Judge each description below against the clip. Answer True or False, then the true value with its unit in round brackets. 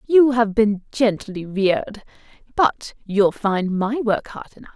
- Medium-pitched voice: False (215 Hz)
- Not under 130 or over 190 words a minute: True (150 wpm)